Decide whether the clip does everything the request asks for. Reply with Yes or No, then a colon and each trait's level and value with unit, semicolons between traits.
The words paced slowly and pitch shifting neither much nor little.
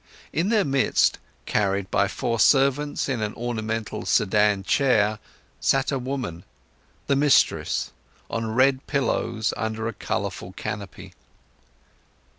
Yes: slow, 115 wpm; average, 4.4 semitones